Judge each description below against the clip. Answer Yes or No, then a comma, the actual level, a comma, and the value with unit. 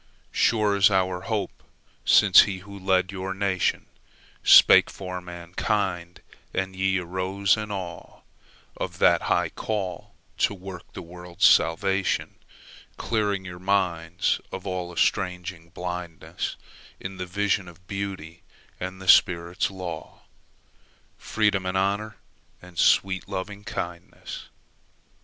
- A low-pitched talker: Yes, very low, 95 Hz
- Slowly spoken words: Yes, slow, 105 wpm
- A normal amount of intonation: No, narrow, 1.9 semitones